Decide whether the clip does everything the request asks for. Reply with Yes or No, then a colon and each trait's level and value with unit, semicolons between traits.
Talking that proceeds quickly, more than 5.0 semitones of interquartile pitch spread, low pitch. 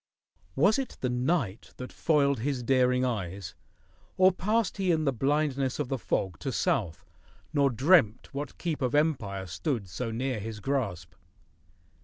No: average, 155 wpm; wide, 5.4 semitones; low, 130 Hz